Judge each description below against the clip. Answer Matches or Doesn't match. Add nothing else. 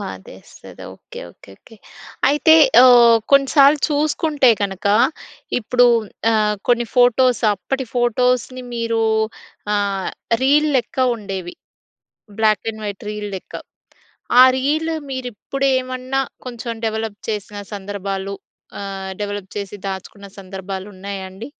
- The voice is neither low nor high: Doesn't match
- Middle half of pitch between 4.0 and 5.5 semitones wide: Matches